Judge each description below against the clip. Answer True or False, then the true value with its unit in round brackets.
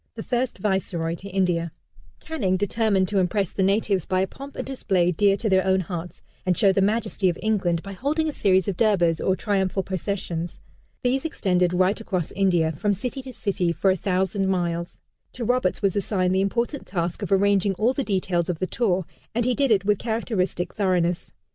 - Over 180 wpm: True (200 wpm)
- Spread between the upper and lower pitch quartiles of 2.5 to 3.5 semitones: True (3.0 semitones)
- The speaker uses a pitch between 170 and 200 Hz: True (190 Hz)